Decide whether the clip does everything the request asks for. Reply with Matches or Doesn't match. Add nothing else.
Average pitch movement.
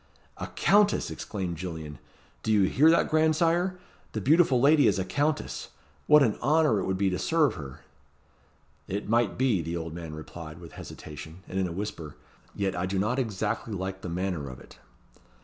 Doesn't match